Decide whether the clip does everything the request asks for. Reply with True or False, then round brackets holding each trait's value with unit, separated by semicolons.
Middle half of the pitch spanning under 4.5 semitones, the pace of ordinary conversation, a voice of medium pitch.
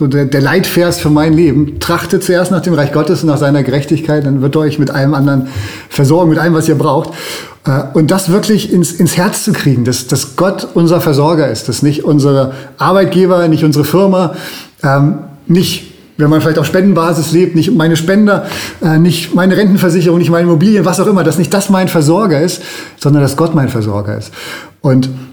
False (3.9 semitones; 195 wpm; 165 Hz)